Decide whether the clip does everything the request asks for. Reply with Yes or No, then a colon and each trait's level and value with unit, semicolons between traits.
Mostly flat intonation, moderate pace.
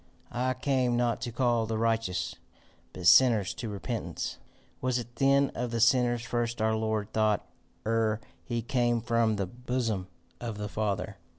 Yes: narrow, 2.0 semitones; average, 160 wpm